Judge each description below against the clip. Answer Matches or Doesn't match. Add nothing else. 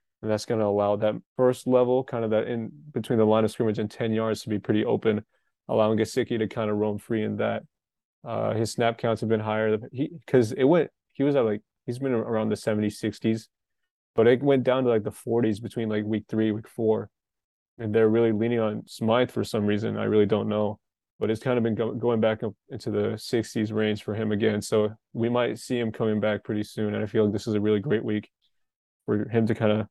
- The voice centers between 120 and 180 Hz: Doesn't match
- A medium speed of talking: Doesn't match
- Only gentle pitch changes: Matches